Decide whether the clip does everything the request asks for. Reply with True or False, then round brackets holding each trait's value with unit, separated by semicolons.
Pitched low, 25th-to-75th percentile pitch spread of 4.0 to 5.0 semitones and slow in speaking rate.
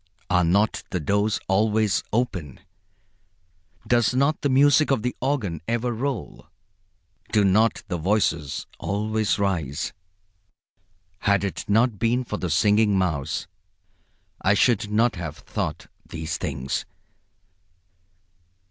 True (105 Hz; 4.7 semitones; 115 wpm)